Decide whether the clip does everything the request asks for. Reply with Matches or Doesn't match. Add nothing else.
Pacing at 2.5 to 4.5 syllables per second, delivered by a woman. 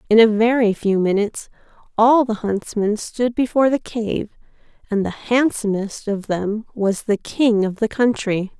Matches